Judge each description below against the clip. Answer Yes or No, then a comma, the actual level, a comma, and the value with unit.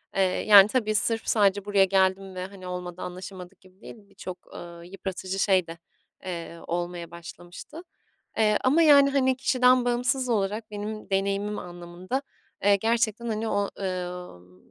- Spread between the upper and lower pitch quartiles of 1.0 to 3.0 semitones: No, average, 3.5 semitones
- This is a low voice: No, high, 195 Hz